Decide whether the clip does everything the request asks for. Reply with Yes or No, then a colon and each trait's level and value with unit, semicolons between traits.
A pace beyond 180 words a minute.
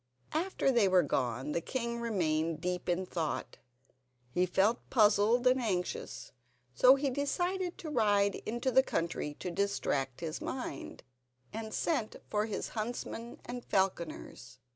No: average, 140 wpm